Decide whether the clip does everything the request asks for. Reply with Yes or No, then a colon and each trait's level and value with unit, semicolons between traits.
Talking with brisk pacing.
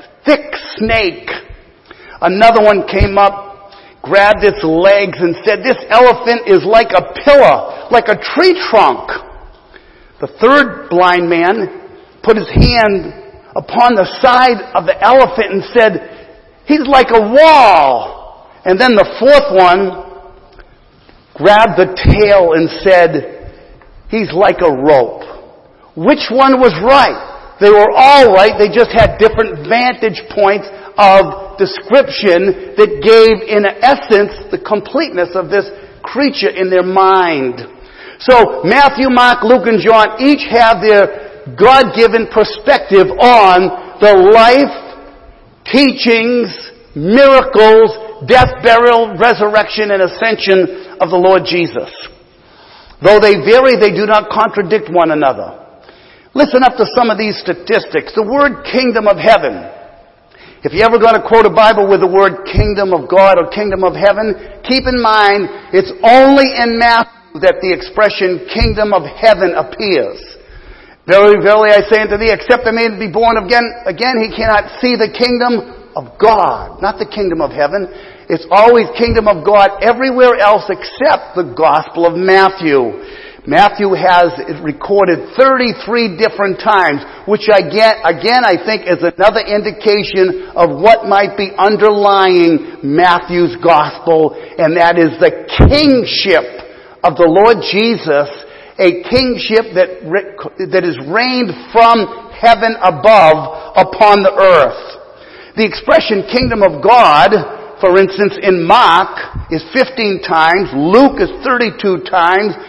No: slow, 135 wpm